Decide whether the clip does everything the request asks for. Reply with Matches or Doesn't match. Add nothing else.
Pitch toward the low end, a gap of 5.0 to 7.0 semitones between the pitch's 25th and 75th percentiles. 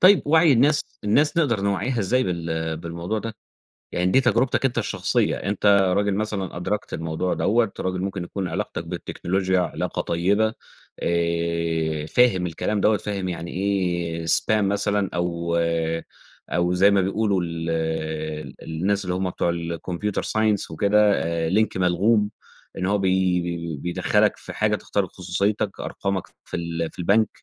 Doesn't match